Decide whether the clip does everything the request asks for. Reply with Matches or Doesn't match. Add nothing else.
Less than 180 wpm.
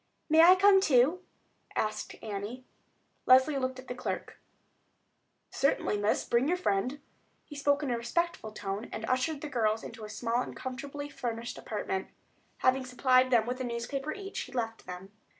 Matches